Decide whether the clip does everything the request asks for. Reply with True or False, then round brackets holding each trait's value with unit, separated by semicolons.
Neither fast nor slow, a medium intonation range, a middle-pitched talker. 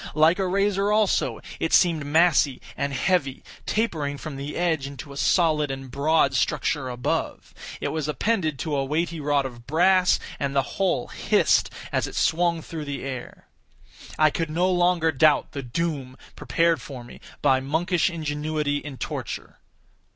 True (160 wpm; 3.6 semitones; 155 Hz)